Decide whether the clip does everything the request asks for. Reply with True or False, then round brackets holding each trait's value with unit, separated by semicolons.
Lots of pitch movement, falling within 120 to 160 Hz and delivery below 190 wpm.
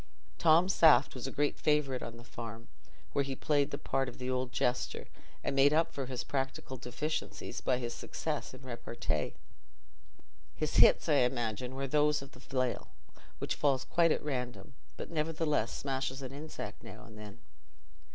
False (3.1 semitones; 135 Hz; 170 wpm)